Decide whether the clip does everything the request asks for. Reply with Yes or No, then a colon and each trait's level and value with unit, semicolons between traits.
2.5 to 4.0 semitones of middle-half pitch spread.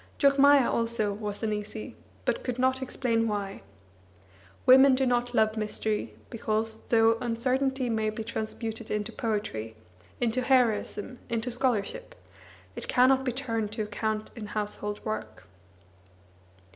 Yes: average, 2.9 semitones